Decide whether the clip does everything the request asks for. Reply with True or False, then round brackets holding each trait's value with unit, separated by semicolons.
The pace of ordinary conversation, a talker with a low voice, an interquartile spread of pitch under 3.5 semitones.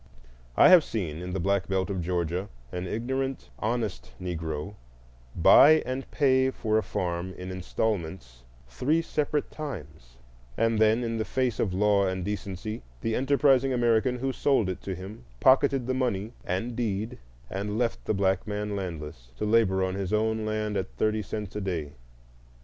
False (165 wpm; 105 Hz; 4.6 semitones)